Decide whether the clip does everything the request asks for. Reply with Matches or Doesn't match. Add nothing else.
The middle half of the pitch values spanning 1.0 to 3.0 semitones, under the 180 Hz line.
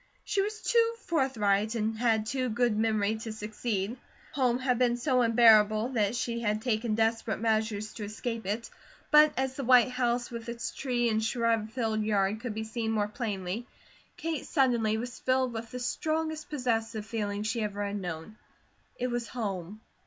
Doesn't match